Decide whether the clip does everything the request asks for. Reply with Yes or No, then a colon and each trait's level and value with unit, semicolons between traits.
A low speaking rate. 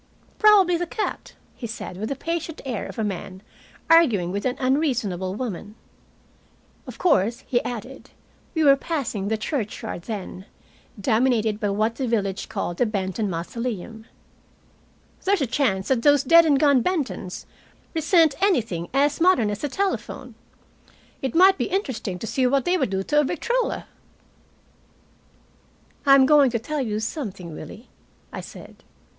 No: average, 150 wpm